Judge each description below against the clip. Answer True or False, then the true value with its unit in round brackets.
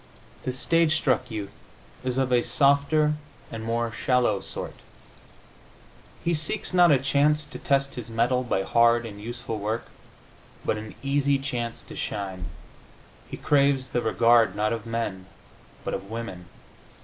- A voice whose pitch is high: False (120 Hz)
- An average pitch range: True (3.7 semitones)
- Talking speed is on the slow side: False (150 wpm)